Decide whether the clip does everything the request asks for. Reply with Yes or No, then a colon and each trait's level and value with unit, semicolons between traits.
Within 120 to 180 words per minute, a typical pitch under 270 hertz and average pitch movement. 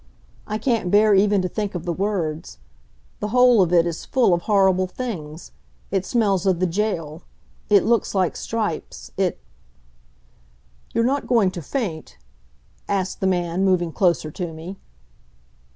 Yes: average, 150 wpm; high, 190 Hz; average, 3.5 semitones